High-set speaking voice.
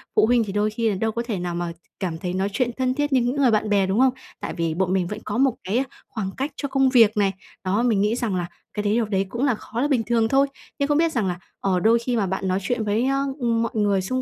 Yes: high, 220 Hz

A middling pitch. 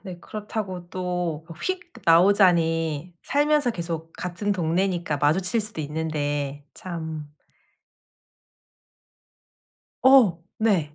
Yes: medium, 175 Hz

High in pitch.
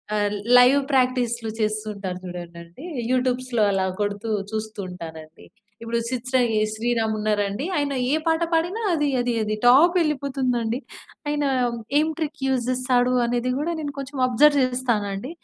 Yes: high, 245 Hz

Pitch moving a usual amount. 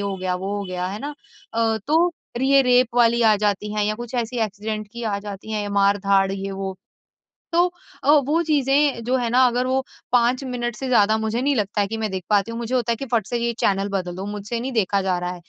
Yes: average, 3.9 semitones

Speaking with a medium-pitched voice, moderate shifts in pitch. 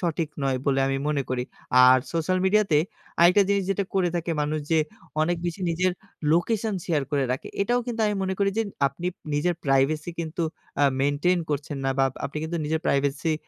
Yes: medium, 165 Hz; average, 4.4 semitones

